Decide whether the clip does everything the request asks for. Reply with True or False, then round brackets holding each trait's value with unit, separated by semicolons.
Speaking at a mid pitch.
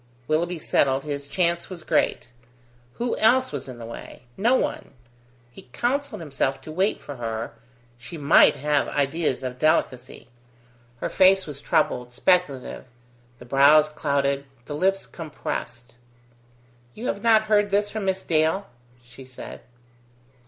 True (155 Hz)